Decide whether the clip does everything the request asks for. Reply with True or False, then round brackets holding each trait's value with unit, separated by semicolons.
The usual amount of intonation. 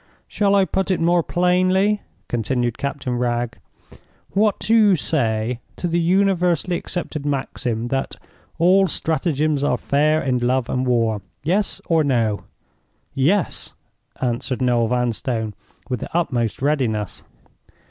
False (6.4 semitones)